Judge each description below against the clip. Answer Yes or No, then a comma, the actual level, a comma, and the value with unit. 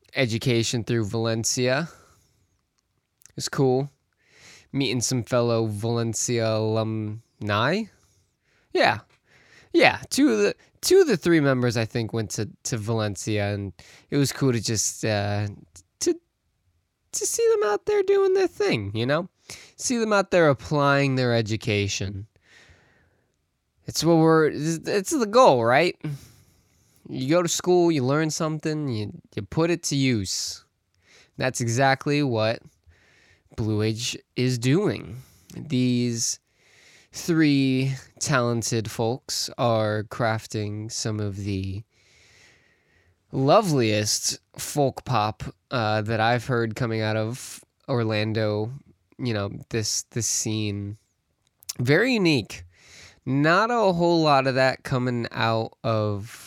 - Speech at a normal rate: No, slow, 120 wpm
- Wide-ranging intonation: No, average, 4.9 semitones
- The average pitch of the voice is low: Yes, low, 120 Hz